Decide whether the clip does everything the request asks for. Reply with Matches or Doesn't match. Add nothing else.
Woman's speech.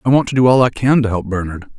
Doesn't match